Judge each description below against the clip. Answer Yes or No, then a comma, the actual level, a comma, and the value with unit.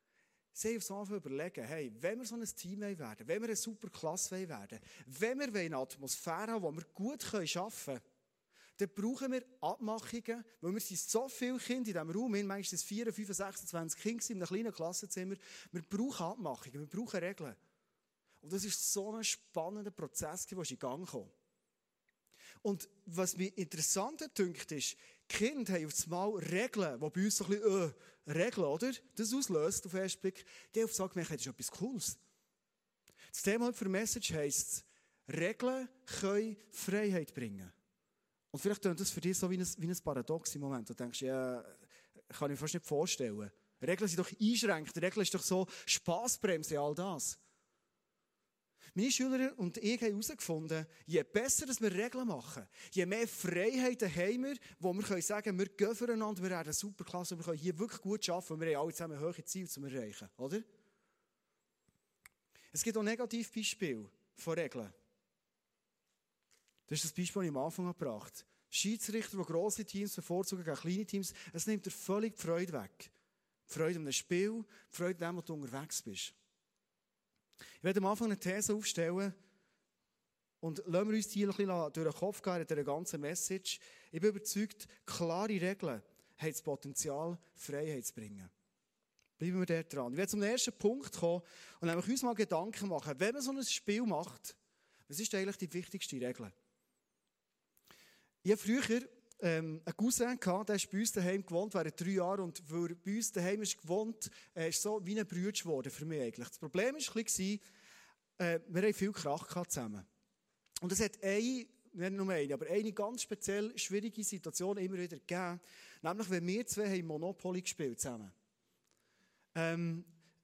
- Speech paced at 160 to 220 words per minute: Yes, average, 175 wpm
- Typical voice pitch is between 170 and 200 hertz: Yes, high, 190 Hz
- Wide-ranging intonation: No, average, 4.3 semitones